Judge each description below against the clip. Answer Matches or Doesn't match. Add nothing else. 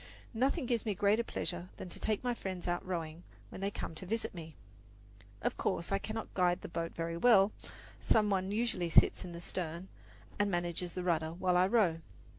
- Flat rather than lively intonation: Doesn't match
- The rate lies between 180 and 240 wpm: Matches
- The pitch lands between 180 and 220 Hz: Matches